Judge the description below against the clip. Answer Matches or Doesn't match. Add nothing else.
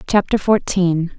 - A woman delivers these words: Matches